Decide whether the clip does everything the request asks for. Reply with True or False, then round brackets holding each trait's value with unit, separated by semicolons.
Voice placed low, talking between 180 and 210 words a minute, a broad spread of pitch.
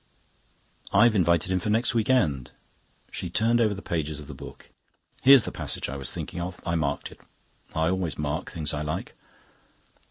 True (85 Hz; 190 wpm; 5.8 semitones)